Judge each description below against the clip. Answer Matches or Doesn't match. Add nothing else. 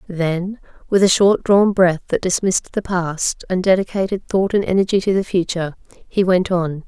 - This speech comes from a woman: Matches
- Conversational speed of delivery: Matches